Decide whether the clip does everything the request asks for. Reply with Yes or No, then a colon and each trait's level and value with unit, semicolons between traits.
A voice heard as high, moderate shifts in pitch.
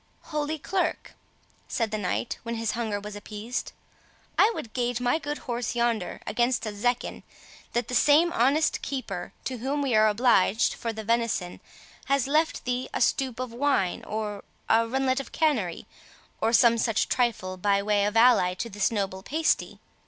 Yes: high, 235 Hz; average, 3.8 semitones